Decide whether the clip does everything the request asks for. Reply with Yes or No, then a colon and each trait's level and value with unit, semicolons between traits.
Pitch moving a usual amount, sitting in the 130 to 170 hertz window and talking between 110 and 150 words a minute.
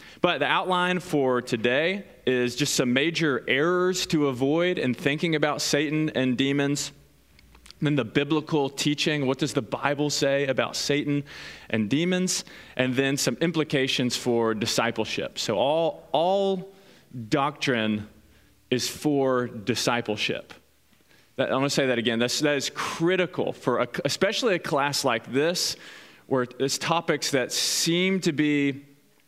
Yes: average, 3.7 semitones; medium, 140 Hz; average, 145 wpm